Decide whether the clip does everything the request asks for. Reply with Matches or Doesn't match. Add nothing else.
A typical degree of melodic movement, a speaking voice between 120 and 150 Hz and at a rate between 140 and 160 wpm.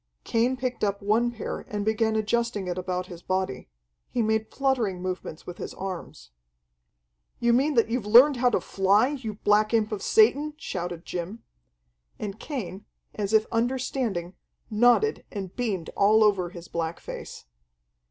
Doesn't match